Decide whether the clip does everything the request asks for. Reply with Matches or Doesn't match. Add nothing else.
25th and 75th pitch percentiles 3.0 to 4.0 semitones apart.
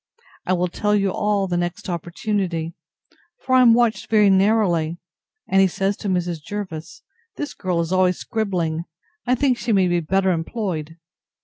Matches